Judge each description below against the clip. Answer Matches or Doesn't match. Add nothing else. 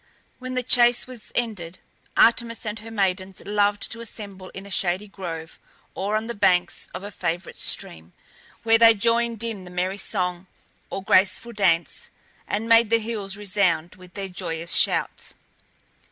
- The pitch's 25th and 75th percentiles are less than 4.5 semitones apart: Matches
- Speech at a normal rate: Matches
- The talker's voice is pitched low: Doesn't match